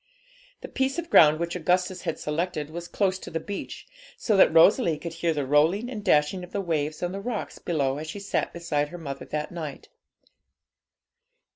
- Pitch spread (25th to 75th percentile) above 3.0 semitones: Yes, average, 3.7 semitones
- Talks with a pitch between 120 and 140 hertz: No, medium, 170 Hz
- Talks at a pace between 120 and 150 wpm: No, average, 190 wpm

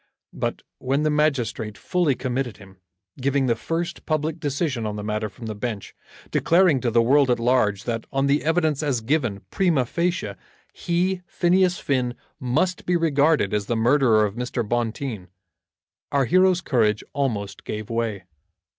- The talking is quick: No, average, 160 wpm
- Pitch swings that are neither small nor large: No, wide, 5.7 semitones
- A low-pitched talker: Yes, low, 130 Hz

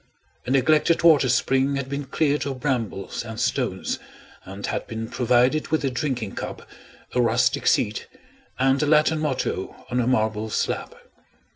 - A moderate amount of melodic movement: Yes, average, 3.6 semitones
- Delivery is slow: No, average, 155 wpm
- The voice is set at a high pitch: No, low, 130 Hz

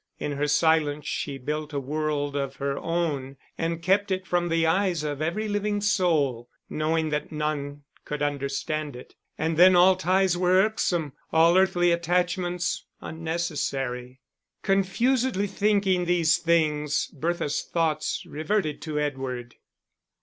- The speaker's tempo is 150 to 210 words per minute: No, slow, 135 wpm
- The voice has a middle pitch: Yes, medium, 160 Hz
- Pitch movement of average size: Yes, average, 3.6 semitones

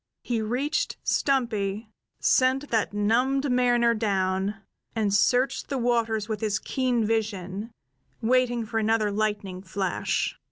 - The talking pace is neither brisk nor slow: No, slow, 120 wpm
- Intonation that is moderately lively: Yes, average, 3.1 semitones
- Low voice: No, high, 225 Hz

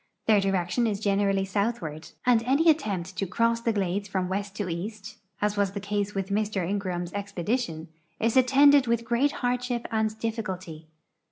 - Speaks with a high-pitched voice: Yes, high, 205 Hz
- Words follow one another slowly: No, average, 165 wpm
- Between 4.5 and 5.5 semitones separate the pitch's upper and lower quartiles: No, average, 3.3 semitones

